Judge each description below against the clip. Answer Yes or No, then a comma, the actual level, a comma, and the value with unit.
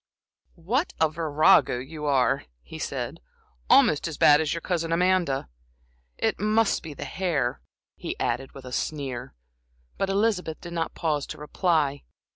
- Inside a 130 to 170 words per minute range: Yes, average, 150 wpm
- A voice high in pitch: No, medium, 160 Hz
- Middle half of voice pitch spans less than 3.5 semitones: No, average, 3.9 semitones